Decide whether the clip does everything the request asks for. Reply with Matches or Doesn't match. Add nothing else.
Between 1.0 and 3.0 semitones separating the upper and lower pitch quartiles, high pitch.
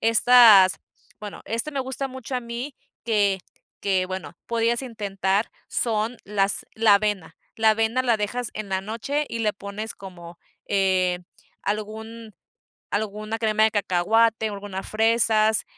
Matches